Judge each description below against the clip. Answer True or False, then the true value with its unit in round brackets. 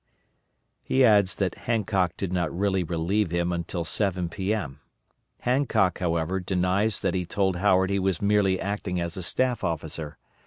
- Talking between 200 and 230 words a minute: False (155 wpm)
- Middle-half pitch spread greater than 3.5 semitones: False (2.7 semitones)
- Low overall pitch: True (95 Hz)